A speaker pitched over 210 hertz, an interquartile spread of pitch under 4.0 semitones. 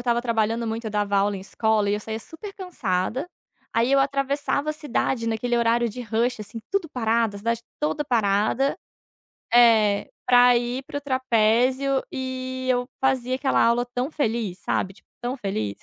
Yes: high, 240 Hz; average, 3.1 semitones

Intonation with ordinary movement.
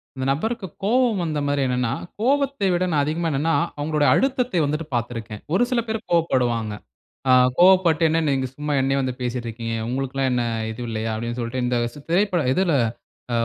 No: wide, 6.8 semitones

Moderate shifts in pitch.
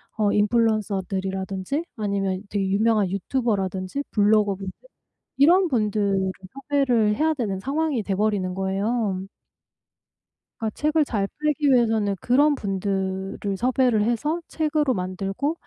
Yes: average, 5.0 semitones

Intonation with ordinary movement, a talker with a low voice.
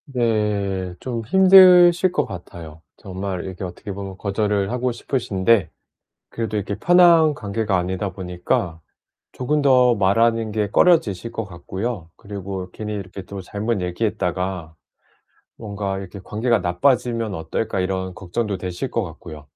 Yes: average, 4.0 semitones; low, 100 Hz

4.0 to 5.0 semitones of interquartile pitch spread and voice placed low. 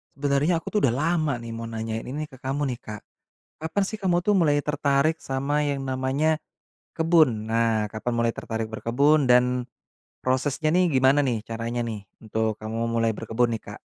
Yes: average, 4.5 semitones; low, 130 Hz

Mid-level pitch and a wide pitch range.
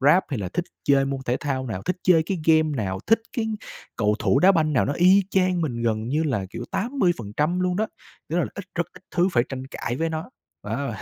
Yes: medium, 155 Hz; wide, 5.9 semitones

